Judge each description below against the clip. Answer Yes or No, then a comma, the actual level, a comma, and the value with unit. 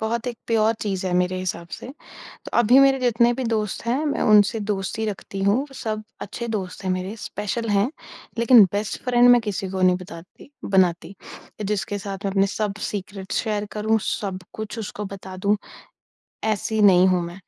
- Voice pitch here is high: Yes, high, 205 Hz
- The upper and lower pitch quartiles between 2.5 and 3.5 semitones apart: Yes, average, 2.9 semitones